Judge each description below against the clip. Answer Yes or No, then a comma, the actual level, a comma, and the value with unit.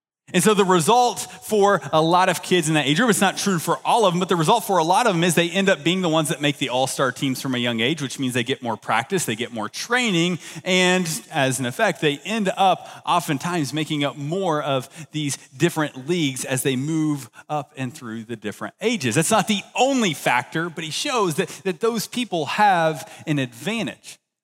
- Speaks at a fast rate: Yes, fast, 230 wpm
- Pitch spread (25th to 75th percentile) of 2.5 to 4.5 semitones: No, average, 5.3 semitones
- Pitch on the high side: No, medium, 160 Hz